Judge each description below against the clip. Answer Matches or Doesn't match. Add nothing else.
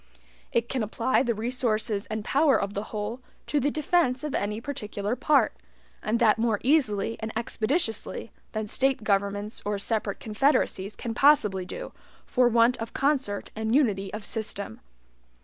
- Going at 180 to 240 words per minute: Doesn't match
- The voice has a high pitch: Matches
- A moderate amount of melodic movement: Matches